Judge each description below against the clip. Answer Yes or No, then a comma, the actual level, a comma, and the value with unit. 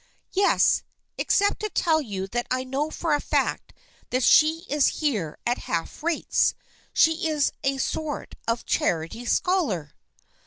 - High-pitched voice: Yes, very high, 285 Hz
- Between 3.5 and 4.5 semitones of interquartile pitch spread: No, wide, 5.6 semitones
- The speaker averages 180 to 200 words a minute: No, average, 155 wpm